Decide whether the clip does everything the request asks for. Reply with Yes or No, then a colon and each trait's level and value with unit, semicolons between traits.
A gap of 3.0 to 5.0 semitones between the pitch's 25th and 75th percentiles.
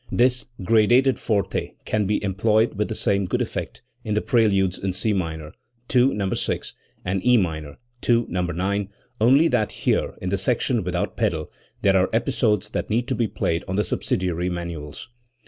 Yes: average, 4.0 semitones